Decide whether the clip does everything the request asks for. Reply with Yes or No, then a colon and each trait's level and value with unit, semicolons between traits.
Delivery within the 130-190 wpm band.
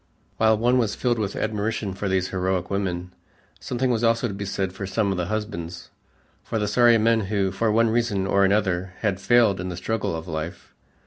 No: fast, 205 wpm